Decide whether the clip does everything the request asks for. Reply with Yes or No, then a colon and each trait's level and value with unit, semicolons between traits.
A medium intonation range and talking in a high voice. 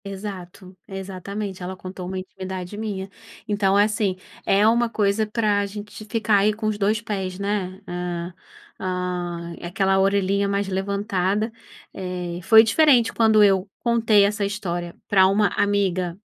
No: narrow, 2.1 semitones; high, 200 Hz